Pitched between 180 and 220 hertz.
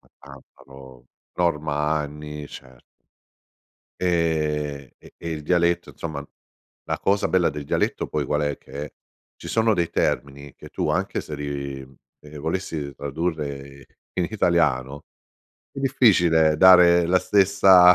No: very low, 75 Hz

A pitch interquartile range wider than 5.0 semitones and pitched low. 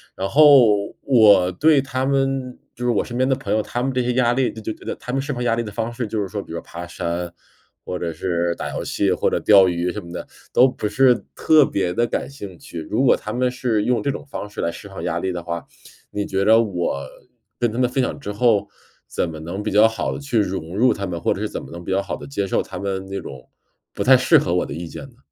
Yes: wide, 5.6 semitones; low, 105 Hz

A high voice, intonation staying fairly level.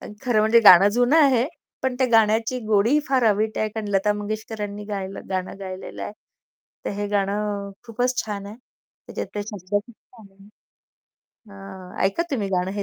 Yes: high, 210 Hz; narrow, 2.3 semitones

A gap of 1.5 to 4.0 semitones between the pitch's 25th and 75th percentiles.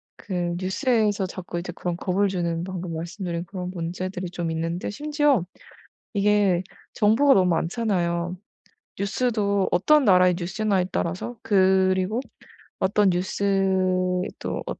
Yes: narrow, 2.6 semitones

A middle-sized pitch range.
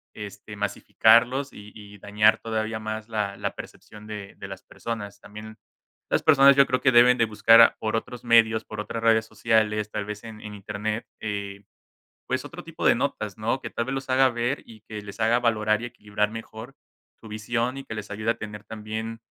No: narrow, 1.8 semitones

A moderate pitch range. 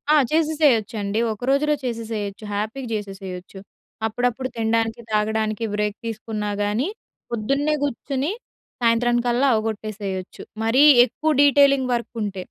Yes: average, 3.7 semitones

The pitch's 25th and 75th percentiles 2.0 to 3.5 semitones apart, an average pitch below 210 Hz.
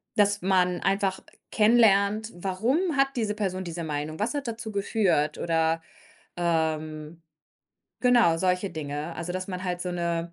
No: average, 4.0 semitones; medium, 185 Hz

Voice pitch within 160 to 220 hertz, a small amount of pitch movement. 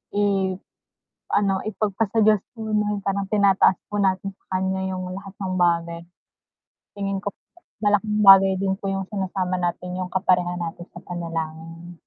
Yes: high, 190 Hz; narrow, 1.9 semitones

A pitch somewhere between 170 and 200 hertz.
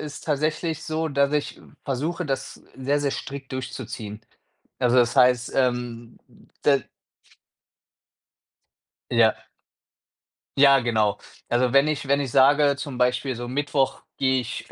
No: low, 135 Hz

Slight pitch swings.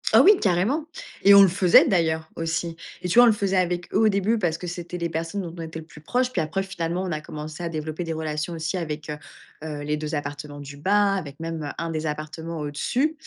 No: average, 3.6 semitones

